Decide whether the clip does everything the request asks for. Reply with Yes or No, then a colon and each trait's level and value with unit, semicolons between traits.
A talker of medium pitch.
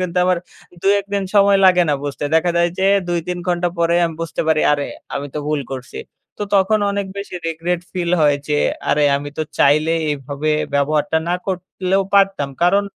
Yes: medium, 170 Hz